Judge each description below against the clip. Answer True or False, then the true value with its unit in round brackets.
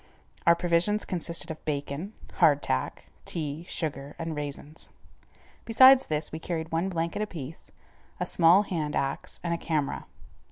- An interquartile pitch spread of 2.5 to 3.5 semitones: True (2.9 semitones)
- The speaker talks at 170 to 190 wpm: False (145 wpm)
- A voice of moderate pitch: True (165 Hz)